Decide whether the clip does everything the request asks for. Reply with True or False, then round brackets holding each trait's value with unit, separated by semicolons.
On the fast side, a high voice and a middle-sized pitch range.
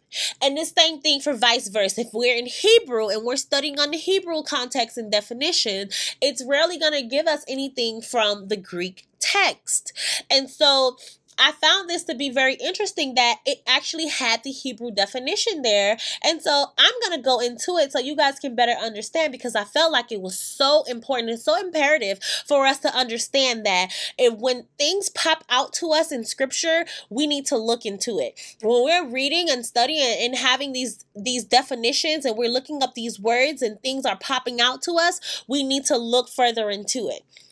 False (195 wpm; 265 Hz; 4.2 semitones)